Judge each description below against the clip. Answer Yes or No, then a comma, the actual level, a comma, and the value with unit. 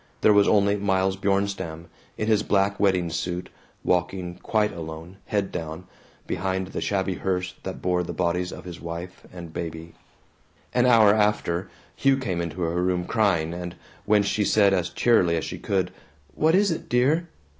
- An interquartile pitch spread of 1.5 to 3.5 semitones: Yes, average, 2.9 semitones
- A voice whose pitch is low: Yes, very low, 95 Hz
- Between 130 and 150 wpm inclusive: No, average, 170 wpm